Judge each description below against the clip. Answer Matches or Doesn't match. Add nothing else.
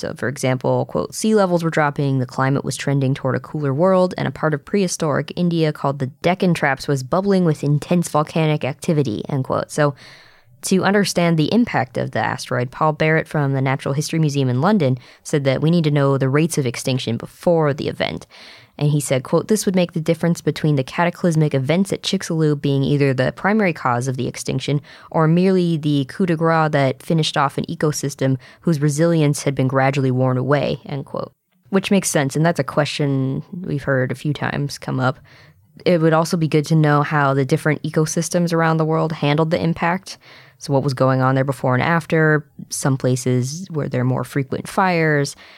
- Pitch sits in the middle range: Matches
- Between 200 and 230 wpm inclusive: Matches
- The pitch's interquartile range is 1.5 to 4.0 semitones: Matches